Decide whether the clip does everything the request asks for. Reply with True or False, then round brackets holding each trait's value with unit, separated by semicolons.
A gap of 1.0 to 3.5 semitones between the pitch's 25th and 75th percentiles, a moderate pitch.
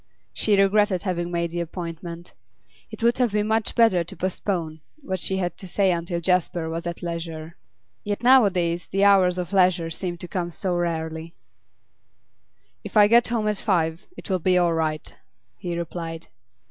True (2.8 semitones; 175 Hz)